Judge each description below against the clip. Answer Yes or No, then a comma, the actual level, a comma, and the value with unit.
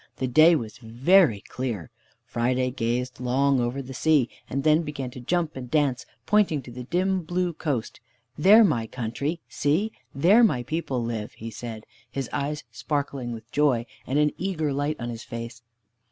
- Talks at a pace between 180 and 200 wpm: No, average, 170 wpm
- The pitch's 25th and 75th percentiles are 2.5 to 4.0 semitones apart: No, average, 4.5 semitones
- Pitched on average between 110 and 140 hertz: Yes, low, 135 Hz